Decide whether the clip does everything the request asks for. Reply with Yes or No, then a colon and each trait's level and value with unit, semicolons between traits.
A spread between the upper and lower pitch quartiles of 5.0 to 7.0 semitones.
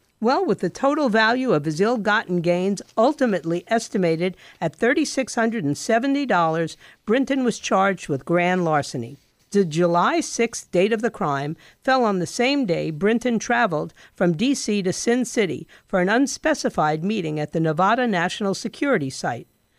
Yes: wide, 5.6 semitones